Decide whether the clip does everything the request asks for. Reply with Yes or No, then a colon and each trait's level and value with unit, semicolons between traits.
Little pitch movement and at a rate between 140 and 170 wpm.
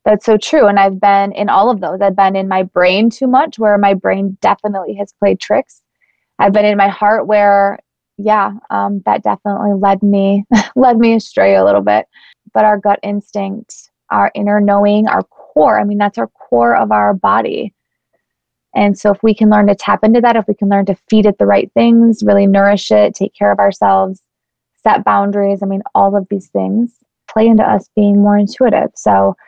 No: narrow, 1.4 semitones; fast, 205 wpm